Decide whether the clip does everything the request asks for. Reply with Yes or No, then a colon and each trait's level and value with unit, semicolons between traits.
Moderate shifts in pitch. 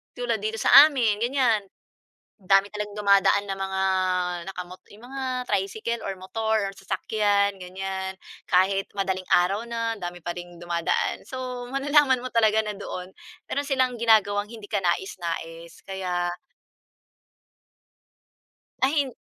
Yes: average, 3.6 semitones